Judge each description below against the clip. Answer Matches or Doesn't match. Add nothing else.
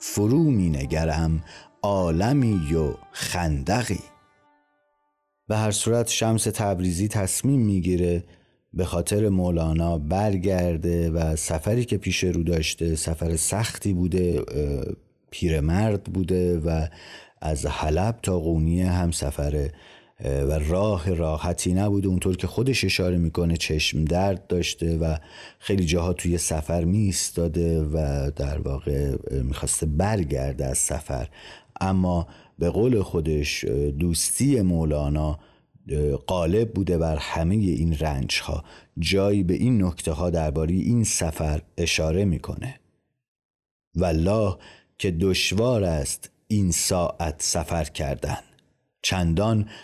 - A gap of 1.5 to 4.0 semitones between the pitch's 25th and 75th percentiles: Matches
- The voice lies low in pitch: Matches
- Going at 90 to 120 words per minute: Matches